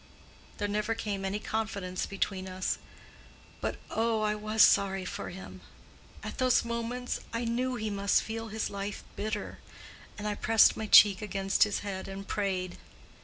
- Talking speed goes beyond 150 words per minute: Yes, average, 160 wpm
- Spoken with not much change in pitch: Yes, narrow, 2.2 semitones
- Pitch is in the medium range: No, high, 210 Hz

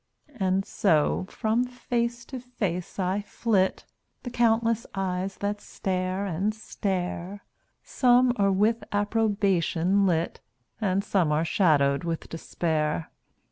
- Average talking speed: No, slow, 115 wpm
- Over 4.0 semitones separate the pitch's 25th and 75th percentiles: No, average, 3.7 semitones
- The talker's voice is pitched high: Yes, high, 195 Hz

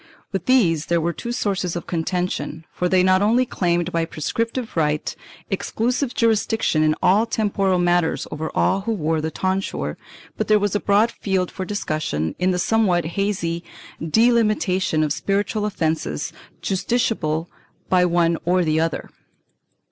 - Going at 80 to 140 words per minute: No, average, 150 wpm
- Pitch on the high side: No, medium, 180 Hz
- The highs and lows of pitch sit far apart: No, average, 4.1 semitones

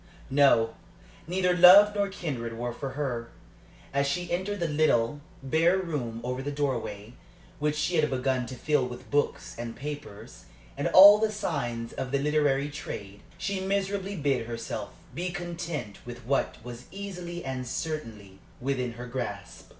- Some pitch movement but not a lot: No, wide, 6.3 semitones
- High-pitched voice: No, medium, 140 Hz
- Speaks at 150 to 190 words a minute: Yes, average, 155 wpm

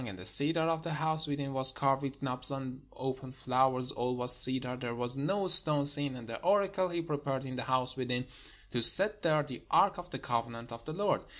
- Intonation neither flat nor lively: Yes, average, 3.9 semitones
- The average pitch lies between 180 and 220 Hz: No, low, 135 Hz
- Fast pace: Yes, fast, 220 wpm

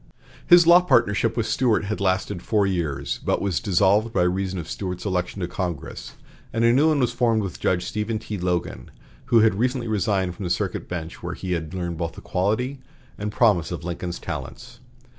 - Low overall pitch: Yes, low, 100 Hz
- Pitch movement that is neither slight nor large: Yes, average, 4.4 semitones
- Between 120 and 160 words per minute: No, average, 195 wpm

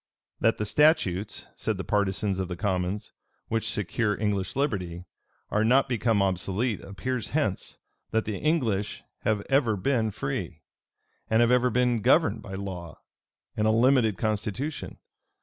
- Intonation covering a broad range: No, average, 4.2 semitones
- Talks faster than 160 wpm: No, average, 145 wpm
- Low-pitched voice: Yes, low, 110 Hz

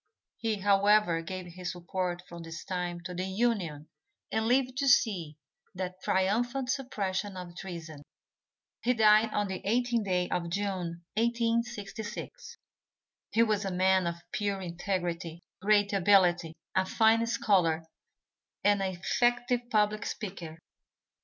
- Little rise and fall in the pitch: No, average, 4.0 semitones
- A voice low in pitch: No, high, 195 Hz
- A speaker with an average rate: No, slow, 130 wpm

